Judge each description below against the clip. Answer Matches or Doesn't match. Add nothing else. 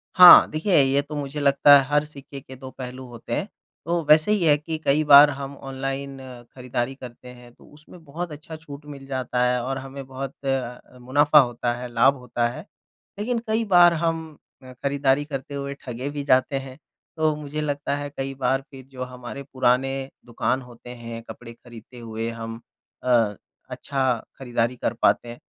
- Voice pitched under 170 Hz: Matches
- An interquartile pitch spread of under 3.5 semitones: Matches